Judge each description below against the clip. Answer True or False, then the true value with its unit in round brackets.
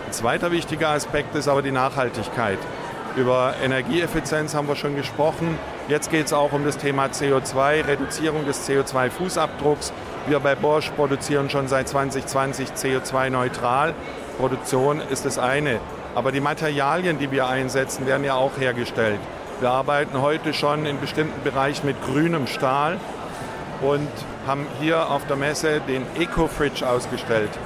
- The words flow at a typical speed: True (145 wpm)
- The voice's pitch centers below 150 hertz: True (140 Hz)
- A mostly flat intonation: True (2.1 semitones)